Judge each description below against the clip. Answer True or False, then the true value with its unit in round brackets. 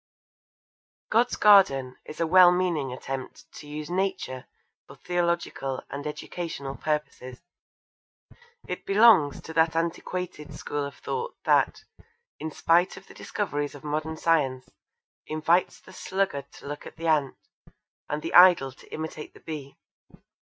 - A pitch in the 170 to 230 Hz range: False (155 Hz)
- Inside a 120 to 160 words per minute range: True (140 wpm)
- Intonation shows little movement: False (3.8 semitones)